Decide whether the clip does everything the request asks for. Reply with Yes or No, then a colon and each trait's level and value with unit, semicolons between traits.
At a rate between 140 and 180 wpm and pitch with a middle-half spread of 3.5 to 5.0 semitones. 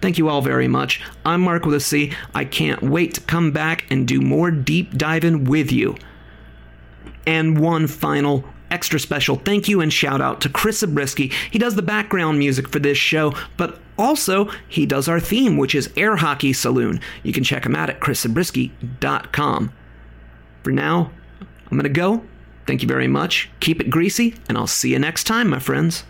No: average, 190 wpm; average, 4.5 semitones